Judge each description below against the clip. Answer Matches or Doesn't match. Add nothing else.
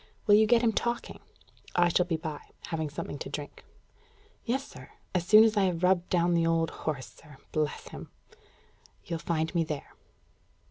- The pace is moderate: Matches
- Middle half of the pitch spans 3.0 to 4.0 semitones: Doesn't match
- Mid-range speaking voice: Matches